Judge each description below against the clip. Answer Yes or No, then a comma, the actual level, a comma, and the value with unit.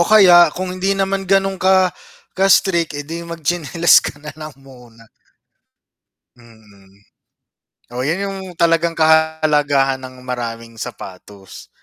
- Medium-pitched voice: Yes, medium, 160 Hz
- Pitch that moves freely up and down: Yes, wide, 6.2 semitones